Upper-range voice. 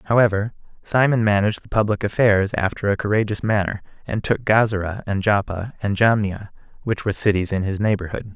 No: low, 105 Hz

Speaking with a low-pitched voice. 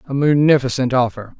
Yes: low, 130 Hz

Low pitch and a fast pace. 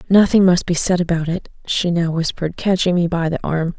No: medium, 175 Hz; fast, 220 wpm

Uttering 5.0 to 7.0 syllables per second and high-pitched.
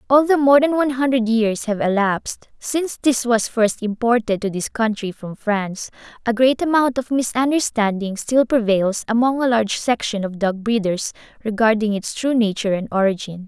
Yes: 5.2 syllables/s; high, 230 Hz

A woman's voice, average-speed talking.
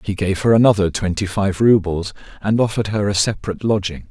No: male; average, 190 wpm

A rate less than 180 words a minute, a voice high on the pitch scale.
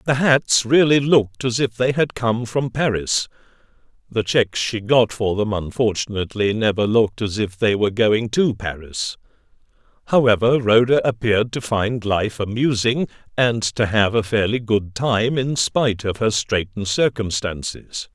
No: average, 155 wpm; low, 115 Hz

